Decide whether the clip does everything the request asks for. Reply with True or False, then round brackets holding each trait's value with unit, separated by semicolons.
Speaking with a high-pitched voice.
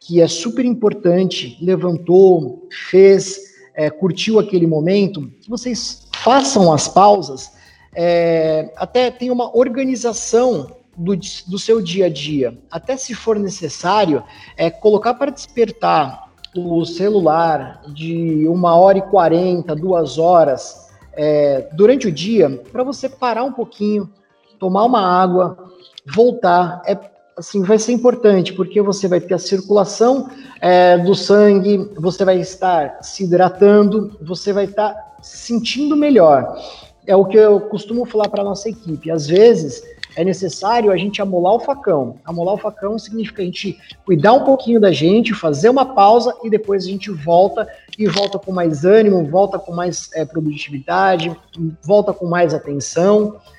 True (195 Hz)